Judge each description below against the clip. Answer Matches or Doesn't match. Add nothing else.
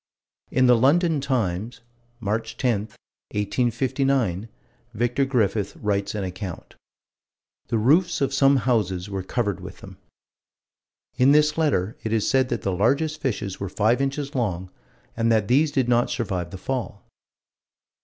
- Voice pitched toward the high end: Doesn't match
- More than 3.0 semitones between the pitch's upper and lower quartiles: Matches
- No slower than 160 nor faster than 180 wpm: Doesn't match